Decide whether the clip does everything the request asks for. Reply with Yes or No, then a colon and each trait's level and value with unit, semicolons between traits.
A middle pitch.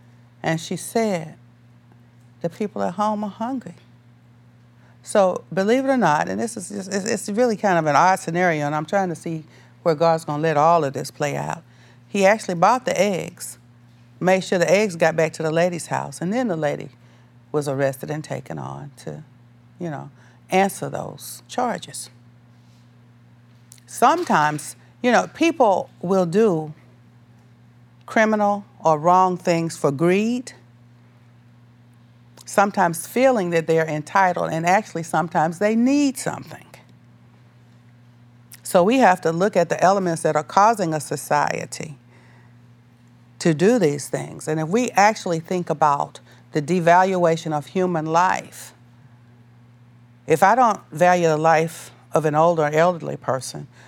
Yes: medium, 155 Hz